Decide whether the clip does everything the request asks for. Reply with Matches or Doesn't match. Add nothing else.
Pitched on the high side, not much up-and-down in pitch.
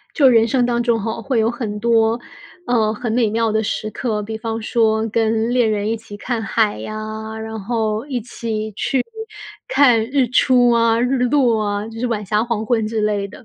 Matches